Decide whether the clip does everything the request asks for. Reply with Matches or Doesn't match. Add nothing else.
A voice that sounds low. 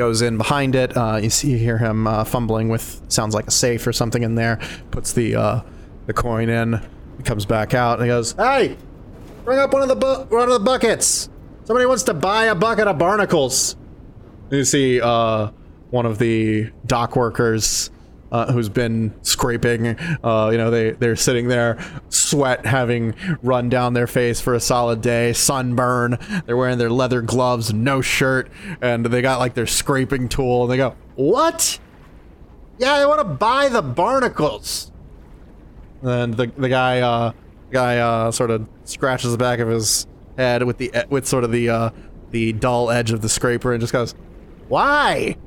Matches